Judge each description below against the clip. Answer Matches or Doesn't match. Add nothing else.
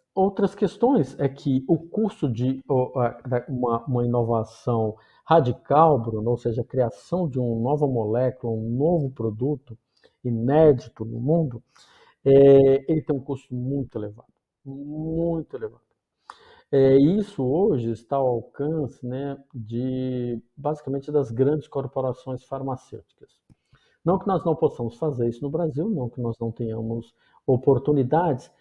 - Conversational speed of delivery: Matches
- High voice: Doesn't match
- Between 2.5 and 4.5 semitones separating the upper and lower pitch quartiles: Matches